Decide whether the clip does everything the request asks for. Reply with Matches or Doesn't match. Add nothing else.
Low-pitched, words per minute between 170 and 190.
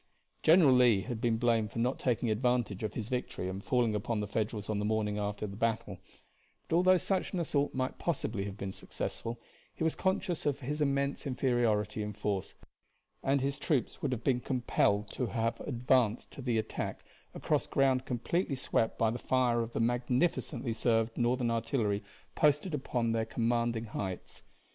Matches